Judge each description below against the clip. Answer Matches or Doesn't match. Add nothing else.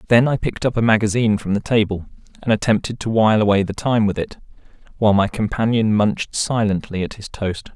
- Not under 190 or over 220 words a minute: Matches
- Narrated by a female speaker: Doesn't match